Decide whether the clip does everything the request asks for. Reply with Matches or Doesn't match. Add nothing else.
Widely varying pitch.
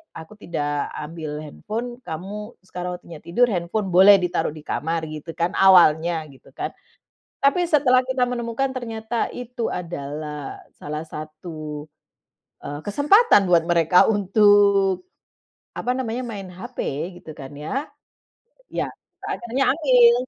Matches